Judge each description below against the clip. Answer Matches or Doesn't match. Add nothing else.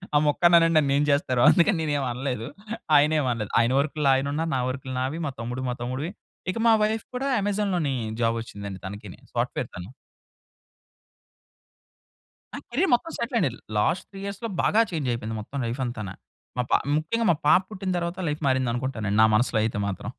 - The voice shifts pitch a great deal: Matches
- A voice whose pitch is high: Doesn't match